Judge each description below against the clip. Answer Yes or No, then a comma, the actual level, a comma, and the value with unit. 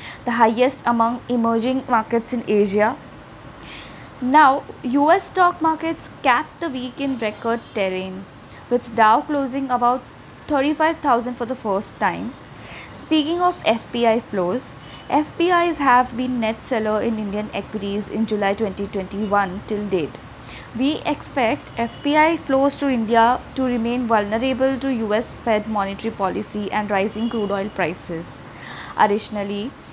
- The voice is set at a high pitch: Yes, high, 230 Hz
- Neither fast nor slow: No, slow, 125 wpm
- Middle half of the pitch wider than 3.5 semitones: Yes, average, 4.3 semitones